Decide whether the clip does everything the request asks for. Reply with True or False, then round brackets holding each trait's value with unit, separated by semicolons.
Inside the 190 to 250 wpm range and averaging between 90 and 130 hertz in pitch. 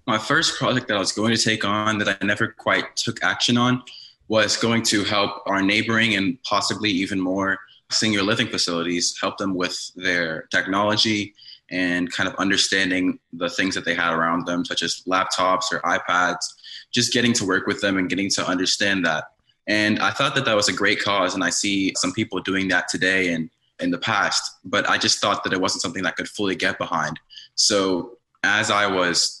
True (205 wpm; 100 Hz)